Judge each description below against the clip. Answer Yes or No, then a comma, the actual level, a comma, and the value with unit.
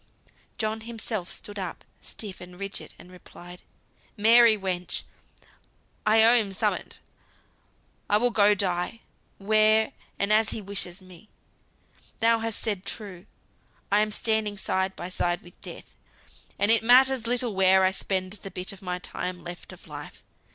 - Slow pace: No, average, 150 wpm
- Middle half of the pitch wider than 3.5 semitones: No, average, 3.0 semitones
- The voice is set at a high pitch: Yes, high, 205 Hz